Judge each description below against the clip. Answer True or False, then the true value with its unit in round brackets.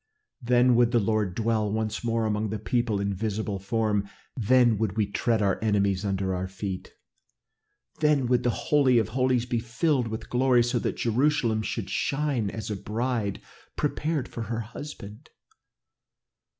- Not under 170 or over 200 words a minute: False (160 wpm)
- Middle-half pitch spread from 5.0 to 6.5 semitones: False (3.1 semitones)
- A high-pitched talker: False (115 Hz)